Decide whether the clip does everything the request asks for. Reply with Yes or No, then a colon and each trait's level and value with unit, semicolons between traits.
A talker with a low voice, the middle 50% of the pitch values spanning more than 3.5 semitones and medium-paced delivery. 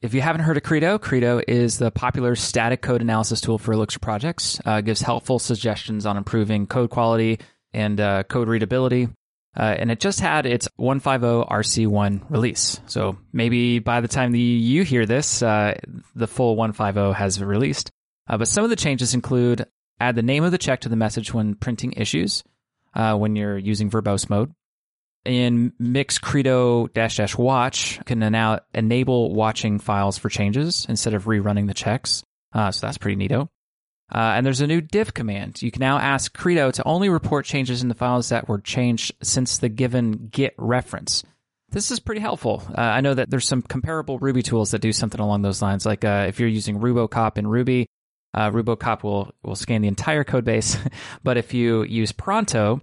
No: low, 115 Hz; average, 2.9 semitones; average, 195 wpm